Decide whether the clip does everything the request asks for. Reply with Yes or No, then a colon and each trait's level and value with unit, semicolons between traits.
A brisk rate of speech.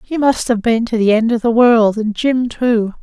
Yes: fast, 260 wpm